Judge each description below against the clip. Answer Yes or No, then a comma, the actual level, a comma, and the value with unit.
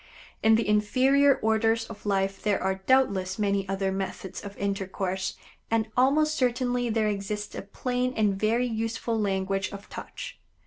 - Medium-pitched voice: No, high, 210 Hz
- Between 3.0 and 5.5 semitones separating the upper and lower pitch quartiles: Yes, average, 3.3 semitones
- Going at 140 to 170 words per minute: Yes, average, 150 wpm